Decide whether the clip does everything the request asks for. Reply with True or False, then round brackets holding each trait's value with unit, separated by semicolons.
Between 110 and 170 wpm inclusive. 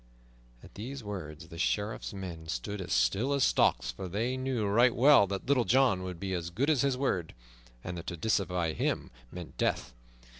False (190 wpm)